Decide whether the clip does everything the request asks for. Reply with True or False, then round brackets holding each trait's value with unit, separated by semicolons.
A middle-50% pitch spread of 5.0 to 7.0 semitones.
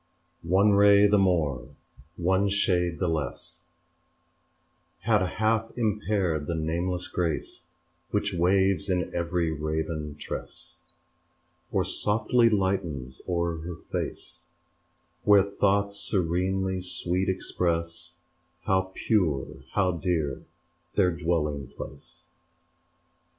False (3.2 semitones)